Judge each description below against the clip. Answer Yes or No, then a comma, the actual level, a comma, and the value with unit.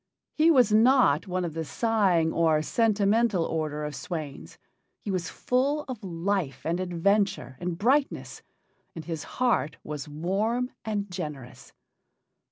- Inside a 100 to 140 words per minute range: Yes, slow, 135 wpm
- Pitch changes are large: Yes, wide, 5.7 semitones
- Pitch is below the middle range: No, medium, 185 Hz